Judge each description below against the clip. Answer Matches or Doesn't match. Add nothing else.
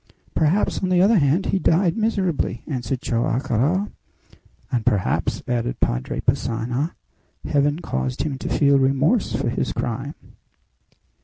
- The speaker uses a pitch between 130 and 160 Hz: Matches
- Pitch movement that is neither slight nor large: Doesn't match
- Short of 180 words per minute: Matches